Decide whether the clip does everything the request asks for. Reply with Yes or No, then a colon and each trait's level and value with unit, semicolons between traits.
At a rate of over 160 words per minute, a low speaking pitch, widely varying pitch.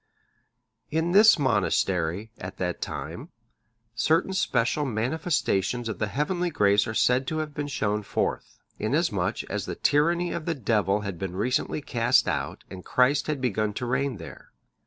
Yes: average, 170 wpm; low, 125 Hz; wide, 6.4 semitones